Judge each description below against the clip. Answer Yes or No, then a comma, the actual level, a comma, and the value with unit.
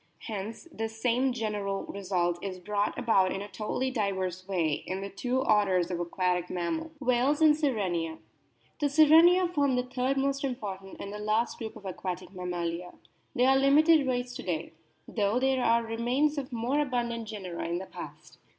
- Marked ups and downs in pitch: Yes, wide, 5.8 semitones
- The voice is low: No, high, 220 Hz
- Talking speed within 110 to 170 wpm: No, average, 180 wpm